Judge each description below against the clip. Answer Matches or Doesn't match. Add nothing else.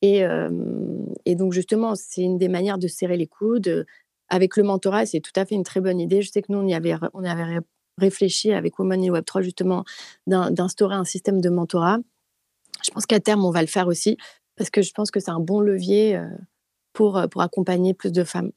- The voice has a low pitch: Doesn't match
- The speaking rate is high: Matches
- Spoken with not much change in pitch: Matches